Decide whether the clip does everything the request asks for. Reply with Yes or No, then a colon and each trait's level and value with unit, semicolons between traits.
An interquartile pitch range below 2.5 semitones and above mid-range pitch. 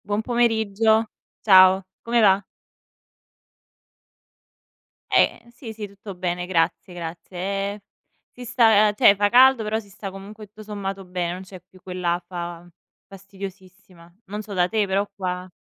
No: average, 2.8 semitones; high, 195 Hz